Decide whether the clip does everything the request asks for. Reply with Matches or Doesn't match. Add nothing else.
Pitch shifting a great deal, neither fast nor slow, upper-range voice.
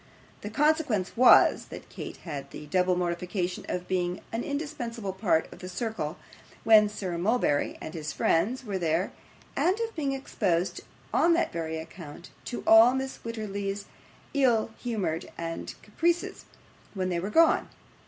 Matches